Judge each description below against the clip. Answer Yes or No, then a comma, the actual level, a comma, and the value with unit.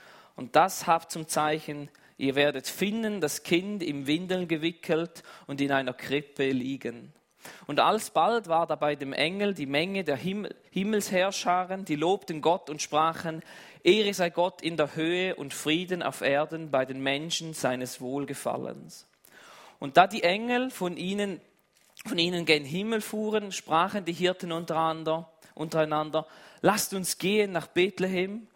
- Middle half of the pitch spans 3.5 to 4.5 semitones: Yes, average, 3.8 semitones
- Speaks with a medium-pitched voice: Yes, medium, 165 Hz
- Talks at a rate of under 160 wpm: Yes, average, 150 wpm